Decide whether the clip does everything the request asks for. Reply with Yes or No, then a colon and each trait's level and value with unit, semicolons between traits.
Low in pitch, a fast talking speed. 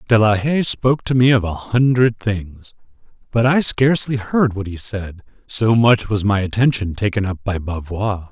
No: low, 110 Hz; average, 190 wpm